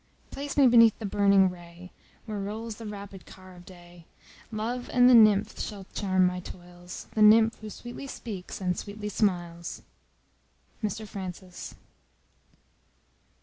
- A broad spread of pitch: No, average, 3.4 semitones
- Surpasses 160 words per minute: No, average, 140 wpm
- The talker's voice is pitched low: No, high, 200 Hz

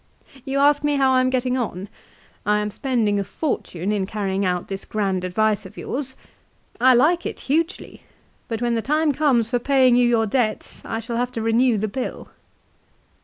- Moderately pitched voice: No, high, 240 Hz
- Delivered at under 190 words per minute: No, average, 195 wpm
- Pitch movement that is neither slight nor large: Yes, average, 4.1 semitones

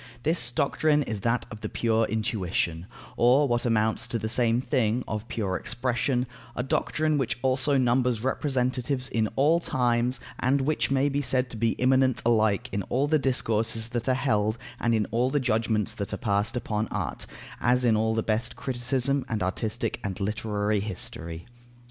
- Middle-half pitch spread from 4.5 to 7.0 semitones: No, average, 3.1 semitones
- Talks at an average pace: Yes, average, 175 wpm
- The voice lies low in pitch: Yes, low, 120 Hz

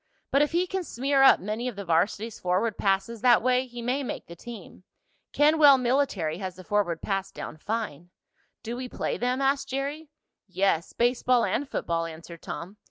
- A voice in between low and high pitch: No, high, 230 Hz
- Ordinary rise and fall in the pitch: No, wide, 6.0 semitones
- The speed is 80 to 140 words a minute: No, average, 180 wpm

